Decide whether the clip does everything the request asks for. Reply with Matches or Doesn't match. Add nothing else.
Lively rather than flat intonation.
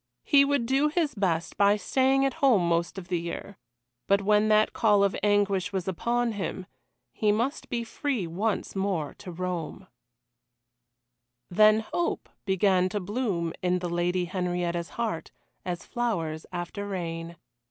Doesn't match